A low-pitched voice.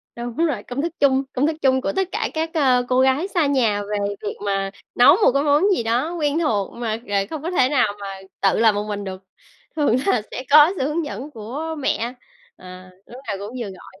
No: very high, 255 Hz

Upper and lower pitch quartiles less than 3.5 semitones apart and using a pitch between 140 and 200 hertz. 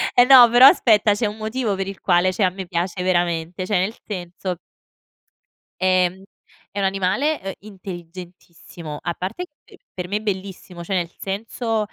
Yes: average, 2.9 semitones; high, 190 Hz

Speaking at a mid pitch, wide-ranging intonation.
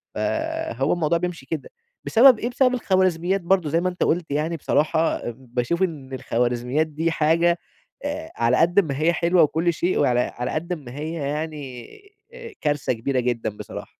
No: medium, 160 Hz; average, 4.4 semitones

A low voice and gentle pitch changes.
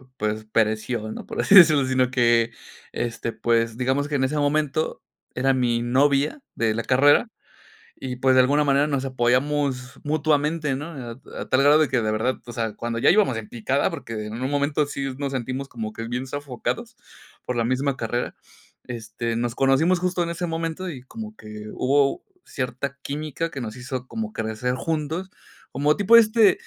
No: low, 130 Hz; average, 3.8 semitones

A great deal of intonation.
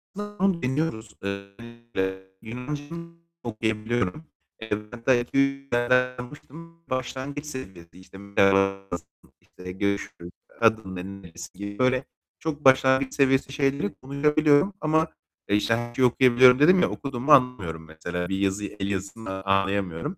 Yes: wide, 5.8 semitones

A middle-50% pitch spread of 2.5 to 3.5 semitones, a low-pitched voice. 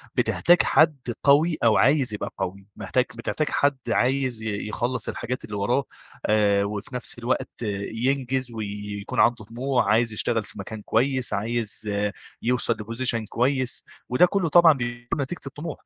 No: average, 3.9 semitones; low, 120 Hz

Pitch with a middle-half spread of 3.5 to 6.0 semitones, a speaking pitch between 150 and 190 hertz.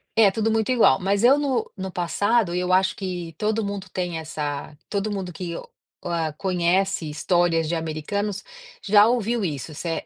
Yes: average, 3.8 semitones; medium, 185 Hz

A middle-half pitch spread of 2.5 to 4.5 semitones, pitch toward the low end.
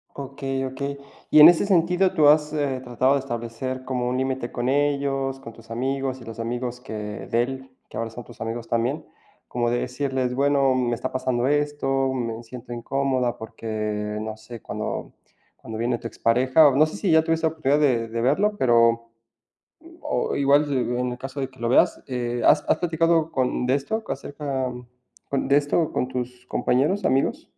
Yes: average, 2.9 semitones; low, 130 Hz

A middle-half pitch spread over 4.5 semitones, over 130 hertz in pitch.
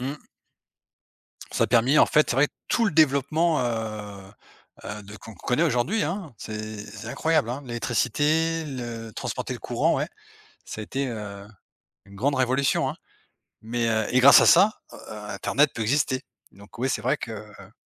No: average, 5.2 semitones; low, 125 Hz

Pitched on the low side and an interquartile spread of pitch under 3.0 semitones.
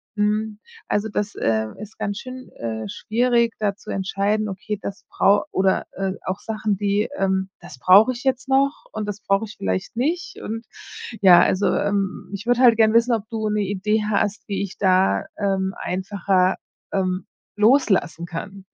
No: high, 205 Hz; narrow, 2.5 semitones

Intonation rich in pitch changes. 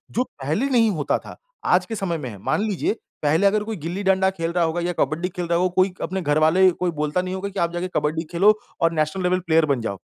No: average, 3.1 semitones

